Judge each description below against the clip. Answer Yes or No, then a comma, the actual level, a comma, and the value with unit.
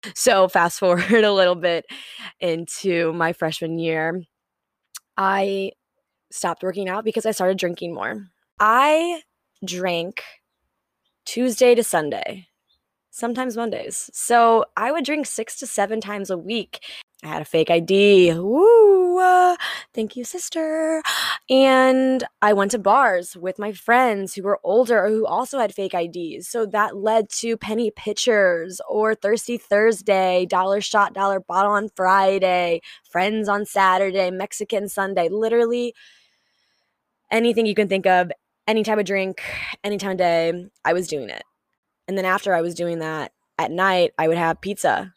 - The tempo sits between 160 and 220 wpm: No, average, 150 wpm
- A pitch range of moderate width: Yes, average, 4.1 semitones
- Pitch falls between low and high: No, high, 200 Hz